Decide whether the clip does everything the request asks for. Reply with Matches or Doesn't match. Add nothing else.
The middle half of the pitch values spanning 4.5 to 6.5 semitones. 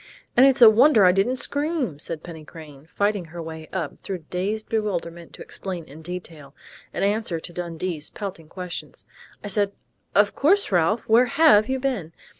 Matches